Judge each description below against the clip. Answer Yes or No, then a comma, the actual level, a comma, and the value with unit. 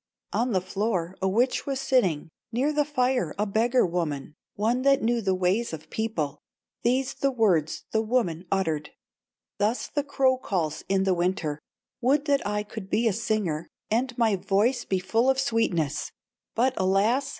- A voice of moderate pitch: No, high, 215 Hz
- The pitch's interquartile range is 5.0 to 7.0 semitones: Yes, wide, 5.6 semitones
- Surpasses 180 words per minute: No, average, 175 wpm